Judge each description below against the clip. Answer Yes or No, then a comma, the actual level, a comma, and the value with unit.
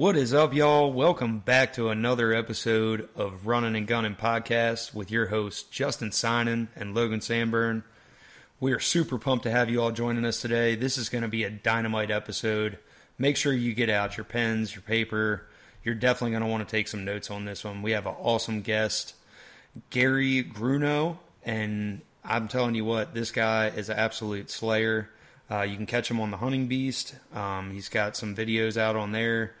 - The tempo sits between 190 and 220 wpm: Yes, average, 195 wpm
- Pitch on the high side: No, low, 115 Hz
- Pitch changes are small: Yes, narrow, 1.9 semitones